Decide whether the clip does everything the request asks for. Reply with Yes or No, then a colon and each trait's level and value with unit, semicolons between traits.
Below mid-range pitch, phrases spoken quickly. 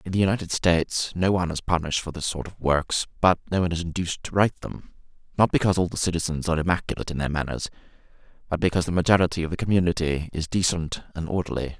Yes: very low, 85 Hz; fast, 215 wpm